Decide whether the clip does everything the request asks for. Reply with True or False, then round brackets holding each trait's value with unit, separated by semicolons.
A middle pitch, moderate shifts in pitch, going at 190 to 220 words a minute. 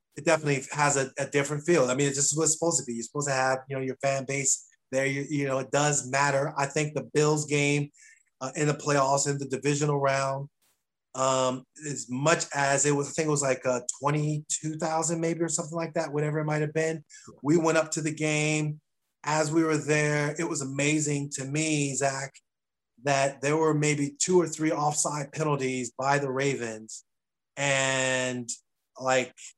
False (145 Hz; 2.1 semitones; 195 wpm)